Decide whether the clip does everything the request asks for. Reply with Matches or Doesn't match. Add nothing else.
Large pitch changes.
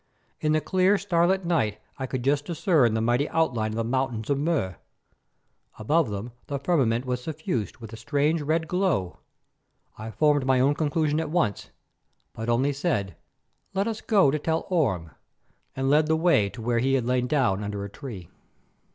Matches